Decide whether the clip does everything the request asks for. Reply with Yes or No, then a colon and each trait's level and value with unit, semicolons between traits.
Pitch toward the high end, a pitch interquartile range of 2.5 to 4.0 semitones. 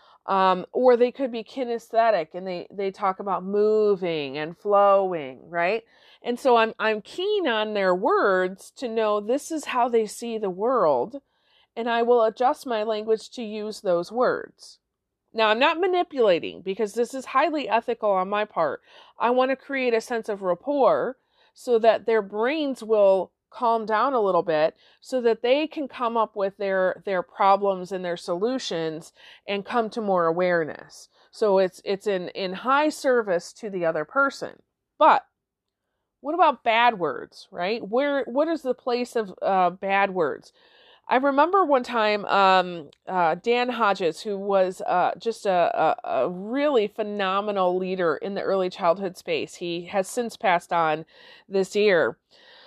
No: high, 215 Hz; average, 4.6 semitones